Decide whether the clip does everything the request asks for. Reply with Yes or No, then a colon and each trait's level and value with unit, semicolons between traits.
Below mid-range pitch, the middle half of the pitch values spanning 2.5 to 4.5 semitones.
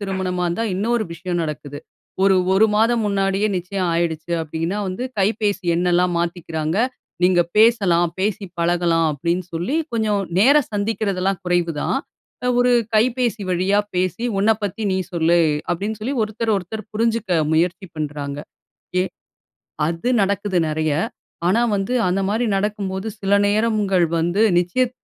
No: high, 190 Hz; average, 3.7 semitones